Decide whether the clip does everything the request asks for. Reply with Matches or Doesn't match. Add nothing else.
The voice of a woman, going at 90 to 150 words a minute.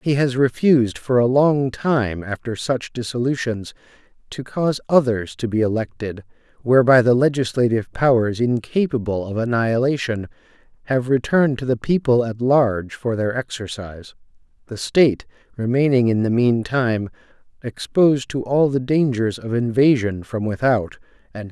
Doesn't match